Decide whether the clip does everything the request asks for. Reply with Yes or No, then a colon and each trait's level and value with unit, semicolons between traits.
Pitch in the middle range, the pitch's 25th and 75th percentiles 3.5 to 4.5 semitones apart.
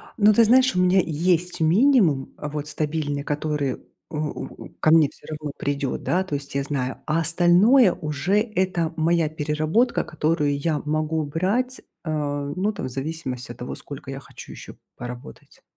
Yes: medium, 155 Hz; average, 3.9 semitones